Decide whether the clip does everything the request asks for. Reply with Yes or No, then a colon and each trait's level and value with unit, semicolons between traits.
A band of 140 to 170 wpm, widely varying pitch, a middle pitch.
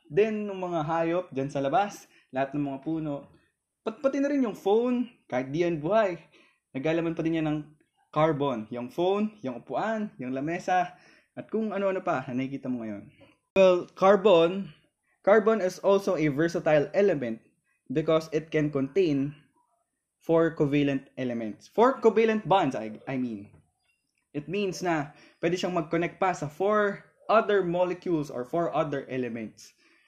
Yes: average, 150 wpm; wide, 5.8 semitones; medium, 165 Hz